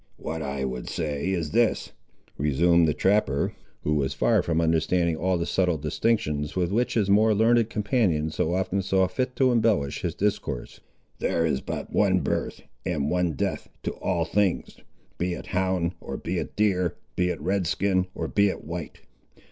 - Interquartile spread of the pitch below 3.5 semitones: No, average, 4.1 semitones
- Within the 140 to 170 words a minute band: No, average, 180 wpm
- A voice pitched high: No, very low, 90 Hz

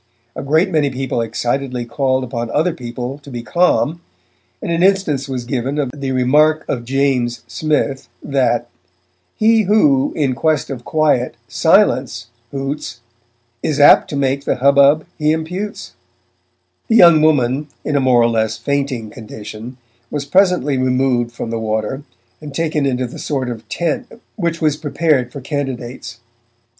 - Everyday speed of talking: Yes, average, 150 wpm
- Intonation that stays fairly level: No, average, 3.7 semitones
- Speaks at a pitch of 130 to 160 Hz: Yes, low, 135 Hz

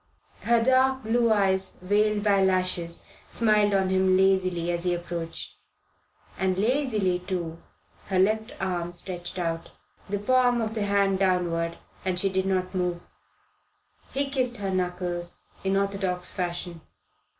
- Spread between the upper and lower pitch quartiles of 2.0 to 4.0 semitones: Yes, average, 2.8 semitones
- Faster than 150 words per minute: No, average, 140 wpm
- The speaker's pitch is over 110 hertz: Yes, high, 190 Hz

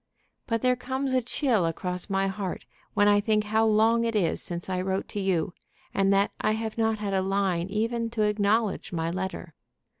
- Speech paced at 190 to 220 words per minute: Yes, average, 200 wpm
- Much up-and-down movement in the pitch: No, average, 2.9 semitones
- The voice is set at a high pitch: Yes, high, 205 Hz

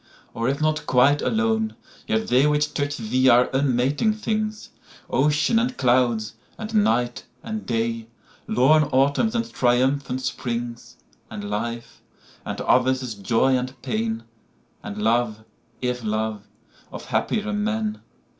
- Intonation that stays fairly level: No, average, 5.0 semitones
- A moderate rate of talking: No, slow, 110 wpm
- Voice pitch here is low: Yes, low, 130 Hz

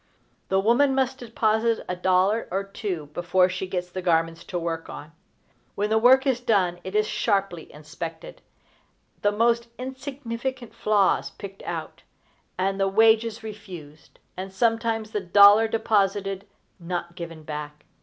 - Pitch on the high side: Yes, high, 195 Hz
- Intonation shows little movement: No, average, 4.1 semitones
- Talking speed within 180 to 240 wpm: No, average, 145 wpm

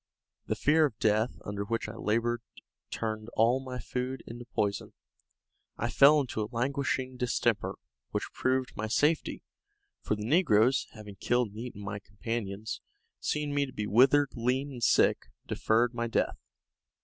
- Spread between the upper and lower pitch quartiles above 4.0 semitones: No, average, 3.4 semitones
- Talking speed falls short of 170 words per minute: Yes, average, 155 wpm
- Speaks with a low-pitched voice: Yes, low, 120 Hz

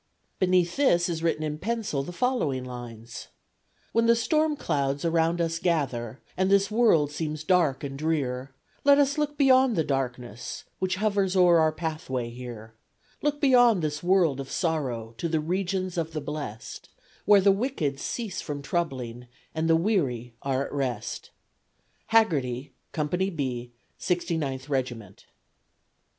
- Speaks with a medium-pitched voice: Yes, medium, 160 Hz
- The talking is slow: No, average, 145 wpm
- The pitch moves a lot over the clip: Yes, wide, 6.0 semitones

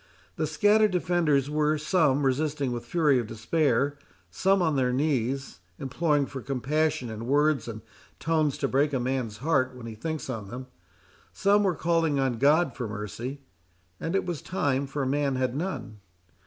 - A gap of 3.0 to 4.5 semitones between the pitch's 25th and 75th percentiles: Yes, average, 3.7 semitones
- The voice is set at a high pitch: No, medium, 140 Hz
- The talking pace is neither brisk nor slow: Yes, average, 170 wpm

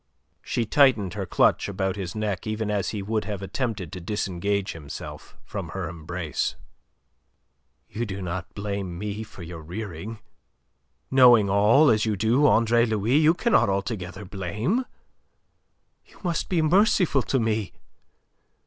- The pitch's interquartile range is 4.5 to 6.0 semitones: No, average, 3.7 semitones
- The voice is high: No, low, 105 Hz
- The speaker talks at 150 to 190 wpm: No, average, 140 wpm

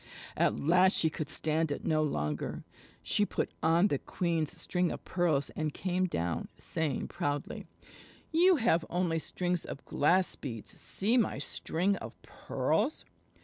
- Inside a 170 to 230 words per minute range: No, average, 145 wpm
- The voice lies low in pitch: No, medium, 165 Hz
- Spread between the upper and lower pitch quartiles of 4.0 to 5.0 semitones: No, average, 3.4 semitones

